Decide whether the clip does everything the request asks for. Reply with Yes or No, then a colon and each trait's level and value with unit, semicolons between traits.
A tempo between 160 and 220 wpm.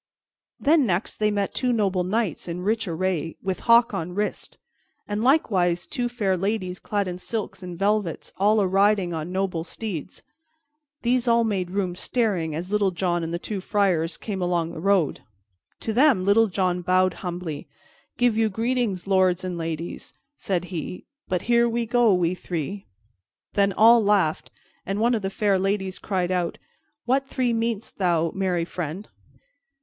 Yes: average, 165 wpm